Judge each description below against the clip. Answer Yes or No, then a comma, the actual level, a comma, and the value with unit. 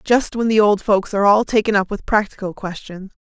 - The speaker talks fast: Yes, fast, 220 wpm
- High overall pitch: Yes, high, 205 Hz